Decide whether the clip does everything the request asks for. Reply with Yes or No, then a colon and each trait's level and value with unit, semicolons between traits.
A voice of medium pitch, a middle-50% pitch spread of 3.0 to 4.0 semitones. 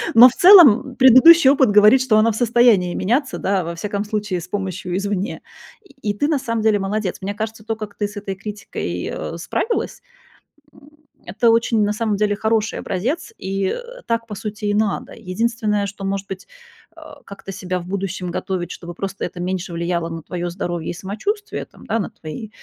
No: high, 210 Hz; average, 3.4 semitones